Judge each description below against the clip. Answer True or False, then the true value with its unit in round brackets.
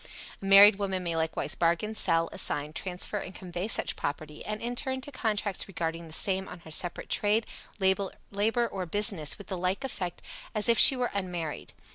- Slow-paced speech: False (180 wpm)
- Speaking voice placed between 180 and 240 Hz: True (190 Hz)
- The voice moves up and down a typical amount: True (3.7 semitones)